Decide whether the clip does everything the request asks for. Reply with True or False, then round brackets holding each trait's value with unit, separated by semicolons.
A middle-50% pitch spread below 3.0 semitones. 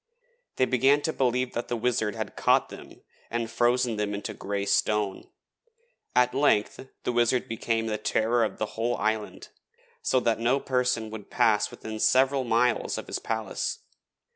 True (2.4 semitones)